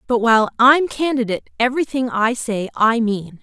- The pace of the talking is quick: No, average, 160 wpm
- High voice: Yes, high, 240 Hz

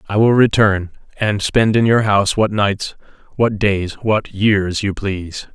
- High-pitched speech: No, low, 105 Hz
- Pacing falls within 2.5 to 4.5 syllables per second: Yes, 4.1 syllables/s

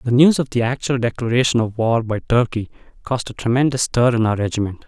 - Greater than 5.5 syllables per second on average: Yes, 6.0 syllables/s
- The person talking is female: No, male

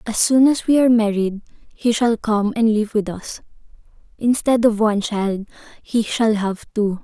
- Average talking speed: Yes, average, 180 wpm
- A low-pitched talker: No, high, 220 Hz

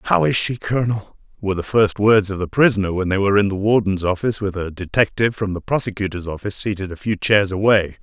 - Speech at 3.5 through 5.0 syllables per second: No, 6.4 syllables/s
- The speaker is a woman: No, male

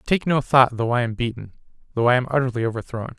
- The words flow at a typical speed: No, fast, 225 wpm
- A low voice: Yes, low, 125 Hz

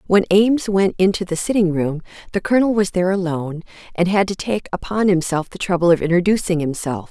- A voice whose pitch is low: No, medium, 185 Hz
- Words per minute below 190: No, average, 195 wpm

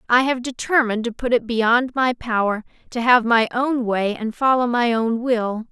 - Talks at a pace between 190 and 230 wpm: Yes, average, 200 wpm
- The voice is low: No, high, 235 Hz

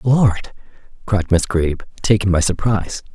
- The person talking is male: Yes, male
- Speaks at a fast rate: No, slow, 135 wpm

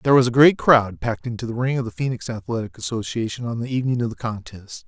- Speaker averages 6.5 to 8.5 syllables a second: Yes, 6.7 syllables/s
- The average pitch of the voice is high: No, low, 120 Hz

